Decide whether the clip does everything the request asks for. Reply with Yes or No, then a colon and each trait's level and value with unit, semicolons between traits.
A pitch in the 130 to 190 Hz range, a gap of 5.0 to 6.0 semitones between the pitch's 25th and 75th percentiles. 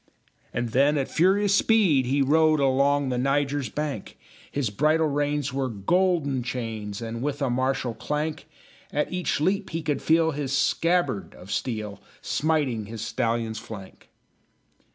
No: medium, 140 Hz; average, 4.4 semitones